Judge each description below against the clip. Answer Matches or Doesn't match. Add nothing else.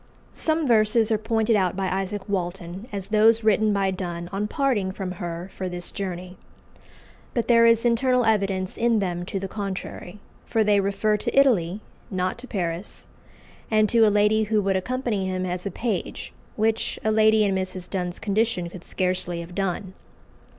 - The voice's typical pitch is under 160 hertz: Doesn't match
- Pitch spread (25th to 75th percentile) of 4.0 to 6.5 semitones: Doesn't match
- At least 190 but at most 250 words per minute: Doesn't match